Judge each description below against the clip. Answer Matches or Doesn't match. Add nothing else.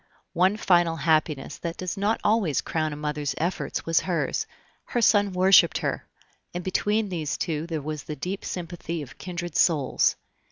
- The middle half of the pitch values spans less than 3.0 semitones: Doesn't match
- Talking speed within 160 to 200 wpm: Matches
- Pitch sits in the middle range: Matches